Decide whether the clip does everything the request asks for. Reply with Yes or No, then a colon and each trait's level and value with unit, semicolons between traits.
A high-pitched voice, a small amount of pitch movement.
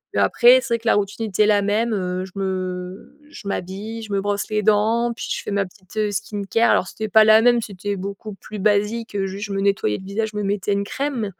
Yes: high, 205 Hz; narrow, 1.9 semitones